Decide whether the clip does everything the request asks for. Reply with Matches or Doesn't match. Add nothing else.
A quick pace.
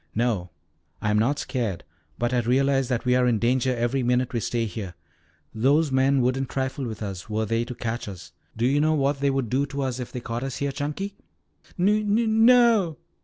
Matches